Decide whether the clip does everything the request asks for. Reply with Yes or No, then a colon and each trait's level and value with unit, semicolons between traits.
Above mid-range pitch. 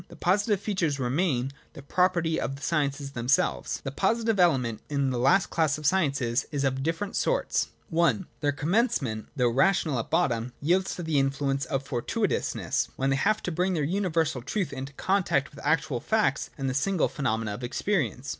No: medium, 145 Hz